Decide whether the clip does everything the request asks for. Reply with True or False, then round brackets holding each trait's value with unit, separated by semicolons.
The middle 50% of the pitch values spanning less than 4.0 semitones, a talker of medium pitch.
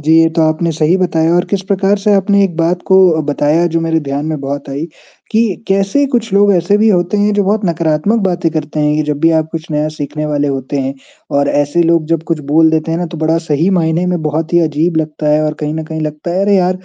True (3.2 semitones; 165 Hz)